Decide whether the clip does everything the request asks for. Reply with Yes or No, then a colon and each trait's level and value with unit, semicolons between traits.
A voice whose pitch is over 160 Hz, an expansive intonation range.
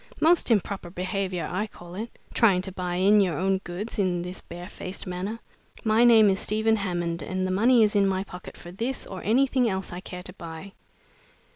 No: high, 190 Hz; average, 3.1 semitones